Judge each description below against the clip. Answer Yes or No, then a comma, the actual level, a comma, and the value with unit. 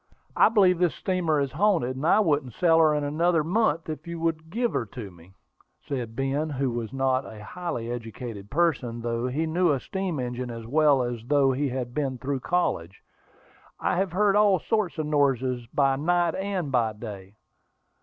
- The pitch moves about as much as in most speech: No, wide, 5.7 semitones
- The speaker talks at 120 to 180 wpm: No, average, 190 wpm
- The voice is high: No, medium, 140 Hz